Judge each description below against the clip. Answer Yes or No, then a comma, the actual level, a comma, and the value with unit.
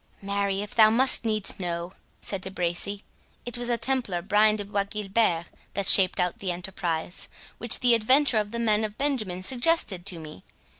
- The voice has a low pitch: No, high, 205 Hz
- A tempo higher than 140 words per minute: Yes, average, 185 wpm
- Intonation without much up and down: No, average, 3.9 semitones